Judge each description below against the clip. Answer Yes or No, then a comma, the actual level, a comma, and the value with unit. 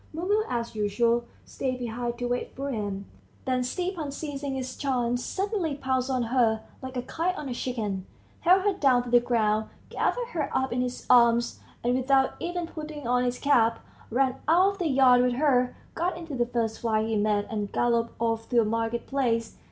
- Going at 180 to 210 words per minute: Yes, average, 195 wpm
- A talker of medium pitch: No, very high, 250 Hz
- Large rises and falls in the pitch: No, average, 3.3 semitones